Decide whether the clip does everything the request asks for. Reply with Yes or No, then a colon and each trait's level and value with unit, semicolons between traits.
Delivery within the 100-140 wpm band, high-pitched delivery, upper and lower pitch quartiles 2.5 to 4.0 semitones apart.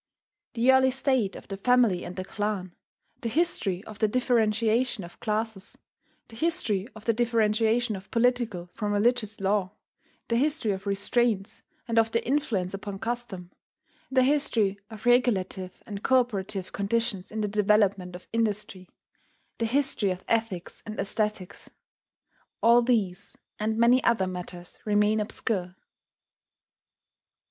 Yes: slow, 135 wpm; high, 215 Hz; average, 3.4 semitones